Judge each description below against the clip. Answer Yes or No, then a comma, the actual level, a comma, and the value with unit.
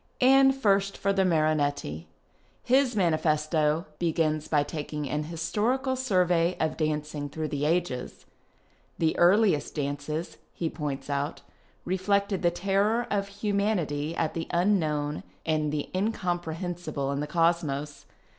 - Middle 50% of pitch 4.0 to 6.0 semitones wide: Yes, average, 4.5 semitones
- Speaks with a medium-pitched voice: Yes, medium, 165 Hz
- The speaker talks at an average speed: No, slow, 125 wpm